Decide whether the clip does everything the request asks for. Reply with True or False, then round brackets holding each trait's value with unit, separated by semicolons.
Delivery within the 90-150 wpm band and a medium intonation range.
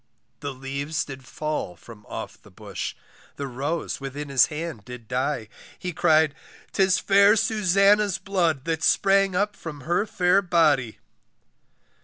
False (140 wpm; 5.9 semitones)